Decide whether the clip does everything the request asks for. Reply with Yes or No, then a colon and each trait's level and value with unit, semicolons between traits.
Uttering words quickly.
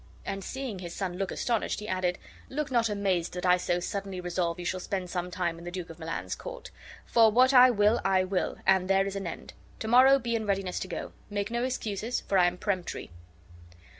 Yes: fast, 220 wpm